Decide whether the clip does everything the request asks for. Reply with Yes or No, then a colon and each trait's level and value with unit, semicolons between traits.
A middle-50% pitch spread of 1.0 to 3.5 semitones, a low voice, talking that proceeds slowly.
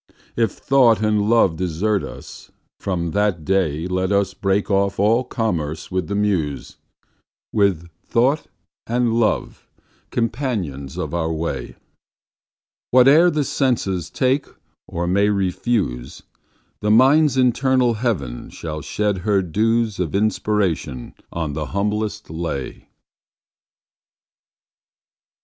No: average, 5.3 semitones; low, 100 Hz; slow, 100 wpm